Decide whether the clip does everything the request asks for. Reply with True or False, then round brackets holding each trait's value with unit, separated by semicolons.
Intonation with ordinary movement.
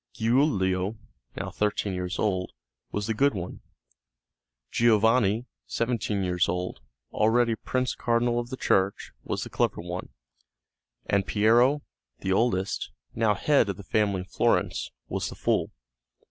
True (3.9 semitones)